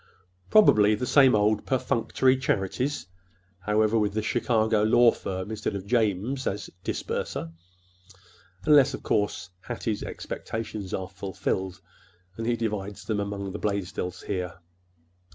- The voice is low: Yes, low, 105 Hz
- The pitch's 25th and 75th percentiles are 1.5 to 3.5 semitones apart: Yes, average, 3.2 semitones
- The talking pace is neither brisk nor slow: No, slow, 120 wpm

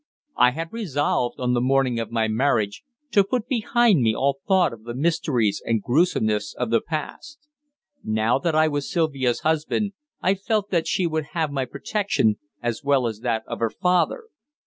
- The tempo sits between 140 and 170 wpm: No, average, 180 wpm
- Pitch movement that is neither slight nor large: No, wide, 7.1 semitones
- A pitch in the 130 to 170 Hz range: Yes, medium, 140 Hz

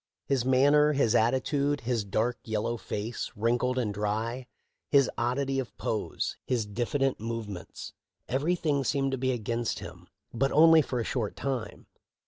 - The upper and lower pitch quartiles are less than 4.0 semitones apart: Yes, average, 3.3 semitones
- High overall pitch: No, low, 125 Hz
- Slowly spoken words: No, average, 155 wpm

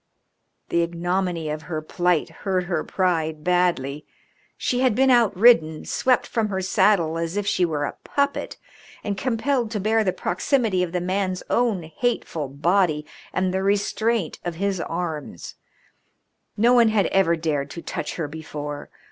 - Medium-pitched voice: Yes, medium, 180 Hz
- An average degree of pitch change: Yes, average, 4.7 semitones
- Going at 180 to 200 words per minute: No, average, 155 wpm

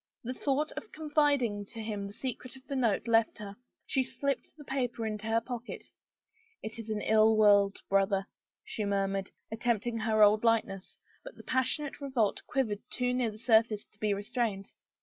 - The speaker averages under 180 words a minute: No, average, 185 wpm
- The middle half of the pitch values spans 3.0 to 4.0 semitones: Yes, average, 3.5 semitones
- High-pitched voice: Yes, high, 225 Hz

